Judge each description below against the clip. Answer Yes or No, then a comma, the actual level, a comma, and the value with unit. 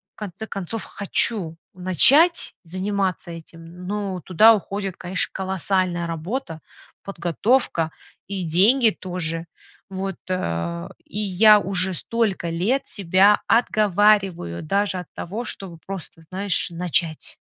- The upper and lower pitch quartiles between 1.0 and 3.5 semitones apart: Yes, average, 3.2 semitones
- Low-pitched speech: No, medium, 185 Hz